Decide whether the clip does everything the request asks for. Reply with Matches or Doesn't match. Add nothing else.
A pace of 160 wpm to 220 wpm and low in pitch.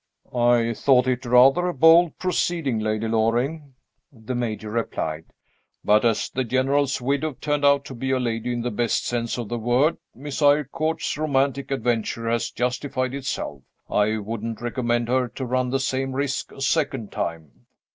Matches